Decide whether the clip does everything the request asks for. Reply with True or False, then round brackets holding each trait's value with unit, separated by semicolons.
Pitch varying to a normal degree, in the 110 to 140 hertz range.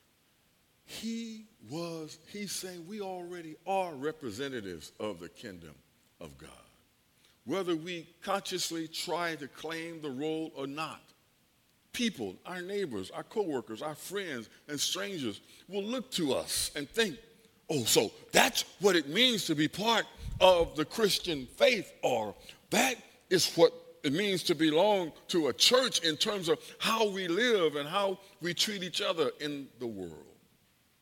False (4.9 semitones; 175 Hz)